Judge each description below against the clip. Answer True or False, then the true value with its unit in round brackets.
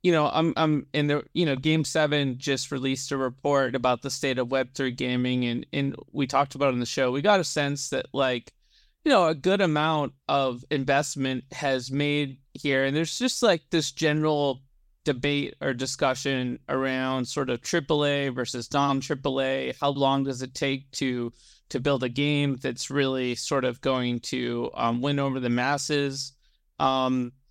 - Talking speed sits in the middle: True (185 wpm)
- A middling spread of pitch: False (1.9 semitones)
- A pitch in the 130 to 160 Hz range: True (135 Hz)